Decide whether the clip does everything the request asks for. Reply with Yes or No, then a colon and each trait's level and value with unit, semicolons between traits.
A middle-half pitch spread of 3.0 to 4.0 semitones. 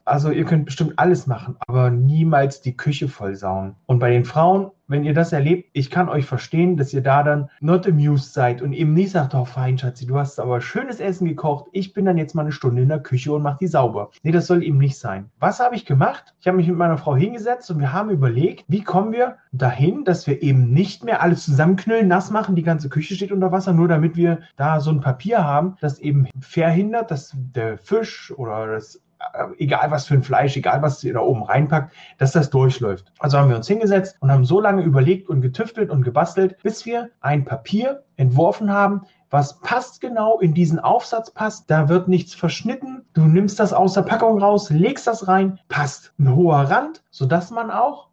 No: wide, 5.5 semitones